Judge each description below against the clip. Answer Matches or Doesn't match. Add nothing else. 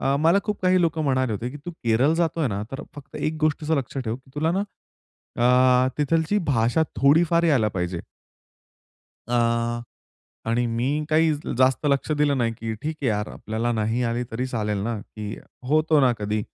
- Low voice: Matches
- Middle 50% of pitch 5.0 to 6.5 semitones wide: Matches